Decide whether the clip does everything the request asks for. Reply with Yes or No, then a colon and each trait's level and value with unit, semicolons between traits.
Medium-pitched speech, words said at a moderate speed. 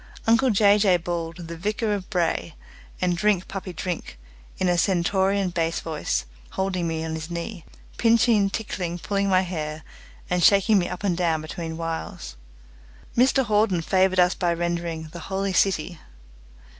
Yes: medium, 180 Hz; average, 155 wpm